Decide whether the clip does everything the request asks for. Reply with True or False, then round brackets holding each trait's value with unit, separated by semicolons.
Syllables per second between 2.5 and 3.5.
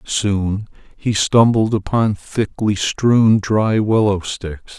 True (3.0 syllables/s)